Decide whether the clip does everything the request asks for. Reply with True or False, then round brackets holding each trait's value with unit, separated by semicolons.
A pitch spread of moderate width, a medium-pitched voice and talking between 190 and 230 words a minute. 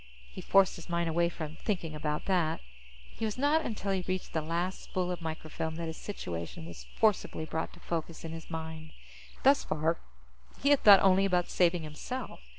True (3.3 semitones; 170 Hz; 195 wpm)